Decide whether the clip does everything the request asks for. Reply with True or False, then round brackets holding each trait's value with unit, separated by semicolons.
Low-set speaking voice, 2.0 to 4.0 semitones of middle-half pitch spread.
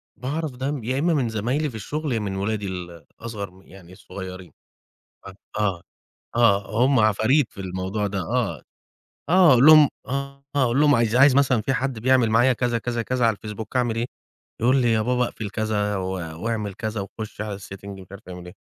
False (115 Hz; 4.5 semitones)